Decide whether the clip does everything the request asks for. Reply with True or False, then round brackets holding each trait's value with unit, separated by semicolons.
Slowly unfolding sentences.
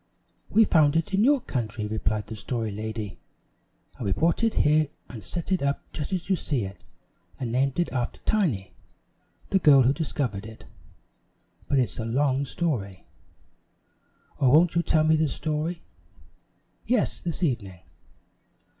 False (155 wpm)